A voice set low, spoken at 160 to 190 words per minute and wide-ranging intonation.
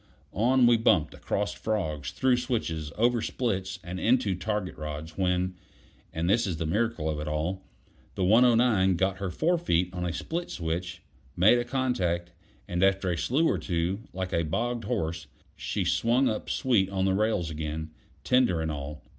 Yes: very low, 95 Hz; average, 170 wpm; wide, 5.7 semitones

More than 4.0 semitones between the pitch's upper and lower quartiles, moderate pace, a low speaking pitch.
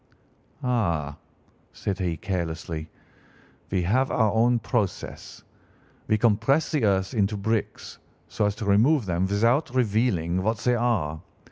No: average, 4.5 semitones; slow, 130 wpm; low, 105 Hz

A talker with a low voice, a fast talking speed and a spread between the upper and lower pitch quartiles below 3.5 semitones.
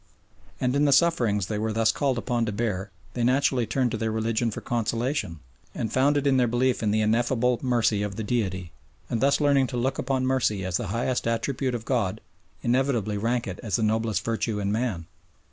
Yes: low, 115 Hz; fast, 210 wpm; average, 3.1 semitones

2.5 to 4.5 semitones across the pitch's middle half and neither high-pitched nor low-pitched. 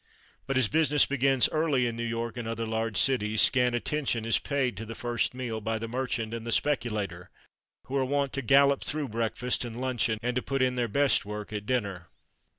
No: average, 3.2 semitones; low, 120 Hz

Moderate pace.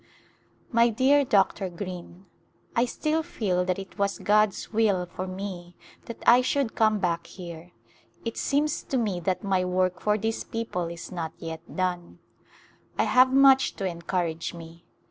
Yes: average, 160 wpm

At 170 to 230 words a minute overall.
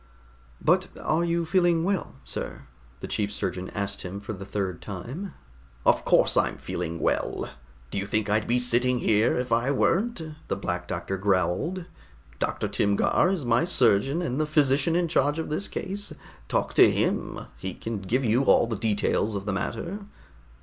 Yes: average, 175 wpm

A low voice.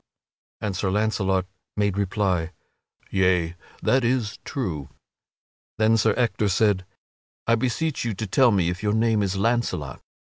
Yes: low, 105 Hz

